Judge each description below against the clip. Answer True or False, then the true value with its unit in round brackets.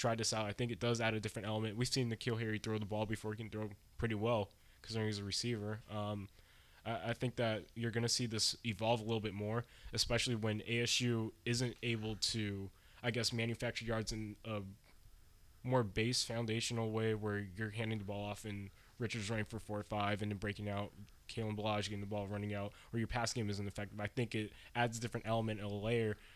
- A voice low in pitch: True (110 Hz)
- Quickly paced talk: True (225 wpm)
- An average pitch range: False (2.0 semitones)